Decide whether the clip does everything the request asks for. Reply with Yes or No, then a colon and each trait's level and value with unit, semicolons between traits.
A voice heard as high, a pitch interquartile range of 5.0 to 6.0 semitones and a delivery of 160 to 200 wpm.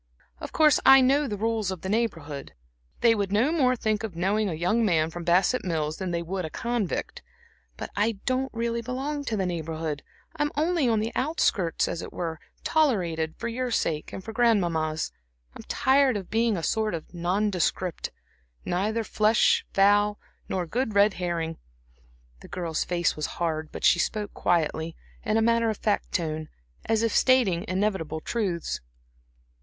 Yes: high, 205 Hz; wide, 5.4 semitones; average, 170 wpm